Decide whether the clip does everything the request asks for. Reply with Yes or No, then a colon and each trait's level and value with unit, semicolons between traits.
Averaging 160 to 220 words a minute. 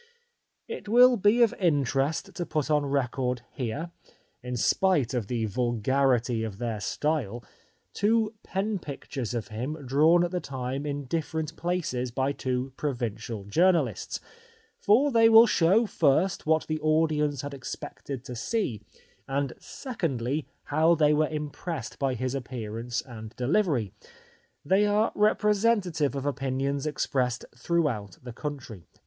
No: average, 140 wpm